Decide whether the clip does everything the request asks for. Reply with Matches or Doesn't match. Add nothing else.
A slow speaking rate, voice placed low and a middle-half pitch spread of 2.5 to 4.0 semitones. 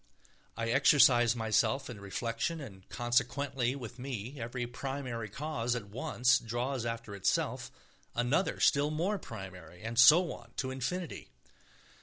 Matches